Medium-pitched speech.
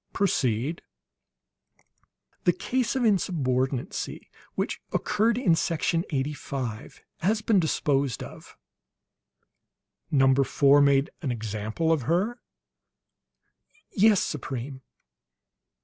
Yes: medium, 145 Hz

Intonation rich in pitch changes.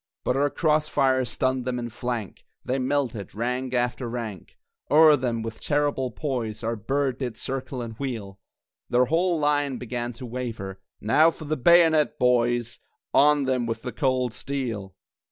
No: average, 3.2 semitones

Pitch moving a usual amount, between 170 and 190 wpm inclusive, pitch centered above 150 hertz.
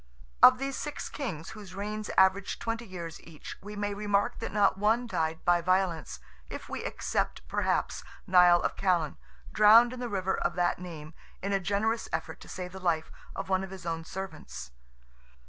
Yes: average, 3.3 semitones; average, 180 wpm; high, 190 Hz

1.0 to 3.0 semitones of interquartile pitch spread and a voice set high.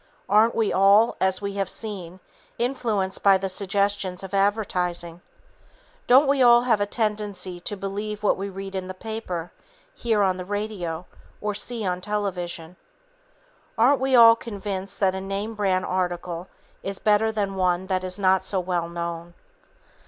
Yes: narrow, 2.4 semitones; high, 195 Hz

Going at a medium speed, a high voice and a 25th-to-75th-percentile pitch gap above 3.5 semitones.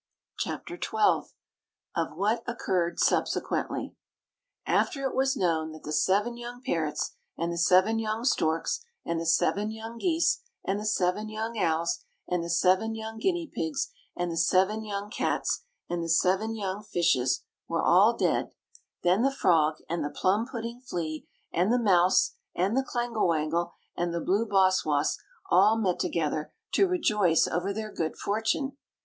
Yes: average, 160 wpm; high, 195 Hz; average, 4.8 semitones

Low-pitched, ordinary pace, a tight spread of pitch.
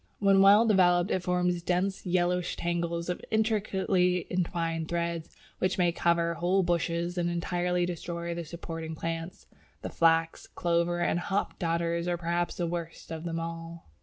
No: medium, 175 Hz; average, 155 wpm; narrow, 1.2 semitones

